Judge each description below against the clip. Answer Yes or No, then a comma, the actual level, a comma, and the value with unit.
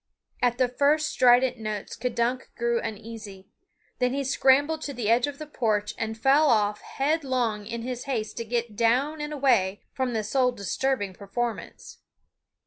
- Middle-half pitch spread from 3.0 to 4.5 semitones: Yes, average, 3.4 semitones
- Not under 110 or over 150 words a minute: No, average, 160 wpm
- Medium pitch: No, high, 240 Hz